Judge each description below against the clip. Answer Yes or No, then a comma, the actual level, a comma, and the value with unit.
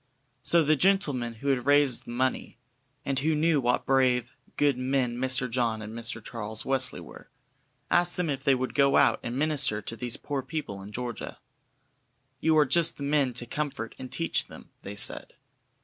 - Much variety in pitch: No, average, 3.4 semitones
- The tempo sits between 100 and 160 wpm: No, average, 185 wpm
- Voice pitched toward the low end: Yes, low, 130 Hz